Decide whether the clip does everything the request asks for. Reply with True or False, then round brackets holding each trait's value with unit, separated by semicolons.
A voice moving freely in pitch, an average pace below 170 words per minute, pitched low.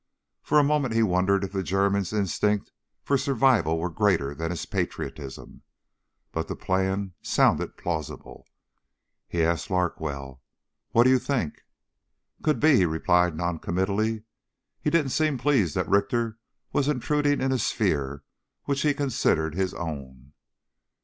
True (7.8 semitones; 140 wpm; 95 Hz)